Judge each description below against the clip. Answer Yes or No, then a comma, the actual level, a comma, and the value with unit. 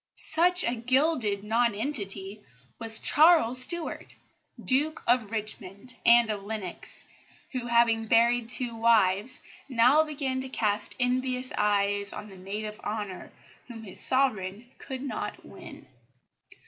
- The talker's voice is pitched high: Yes, high, 230 Hz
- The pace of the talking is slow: Yes, slow, 125 wpm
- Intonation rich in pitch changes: No, average, 3.6 semitones